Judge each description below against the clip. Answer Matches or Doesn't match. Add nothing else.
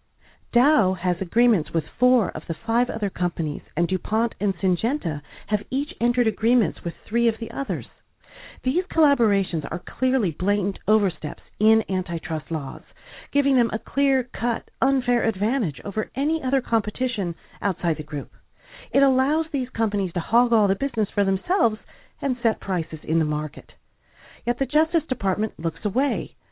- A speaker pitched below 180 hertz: Doesn't match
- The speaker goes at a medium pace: Matches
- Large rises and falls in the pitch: Matches